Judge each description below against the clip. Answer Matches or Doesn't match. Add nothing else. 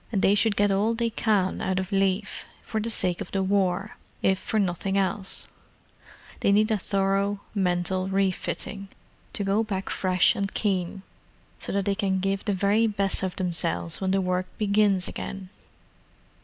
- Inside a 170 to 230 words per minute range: Matches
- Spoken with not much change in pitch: Matches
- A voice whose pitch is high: Matches